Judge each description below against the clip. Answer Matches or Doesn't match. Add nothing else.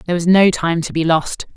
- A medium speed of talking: Doesn't match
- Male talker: Doesn't match